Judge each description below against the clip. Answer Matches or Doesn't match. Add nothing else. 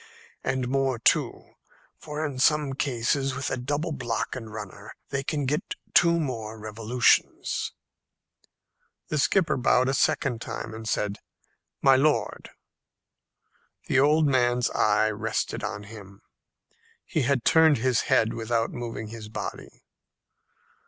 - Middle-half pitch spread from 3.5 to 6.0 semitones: Matches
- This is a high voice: Doesn't match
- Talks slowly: Matches